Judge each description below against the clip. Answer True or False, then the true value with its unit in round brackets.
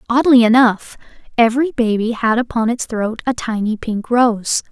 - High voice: True (230 Hz)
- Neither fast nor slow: True (155 wpm)